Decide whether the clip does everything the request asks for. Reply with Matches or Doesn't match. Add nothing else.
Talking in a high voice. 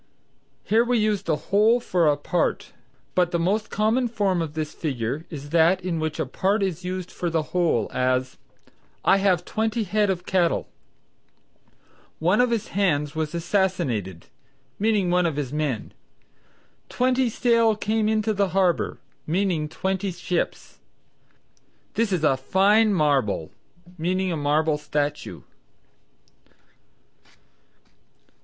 Doesn't match